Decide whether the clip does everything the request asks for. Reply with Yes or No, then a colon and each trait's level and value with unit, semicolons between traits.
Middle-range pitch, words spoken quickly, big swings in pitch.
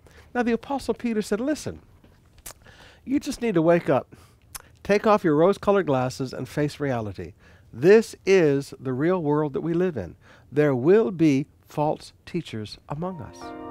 No: medium, 150 Hz; average, 160 wpm; wide, 7.8 semitones